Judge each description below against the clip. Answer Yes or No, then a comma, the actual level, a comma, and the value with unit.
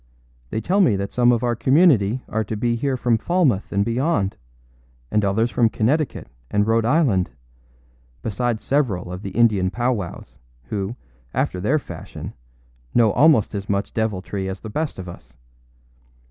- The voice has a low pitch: Yes, low, 110 Hz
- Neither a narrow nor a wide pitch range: Yes, average, 4.0 semitones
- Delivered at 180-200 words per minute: No, average, 160 wpm